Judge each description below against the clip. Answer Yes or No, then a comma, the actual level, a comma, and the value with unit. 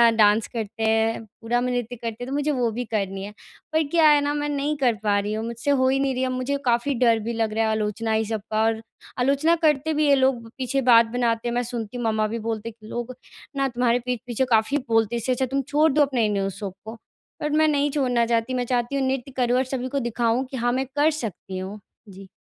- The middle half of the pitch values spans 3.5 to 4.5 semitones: No, average, 3.1 semitones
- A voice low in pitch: No, high, 240 Hz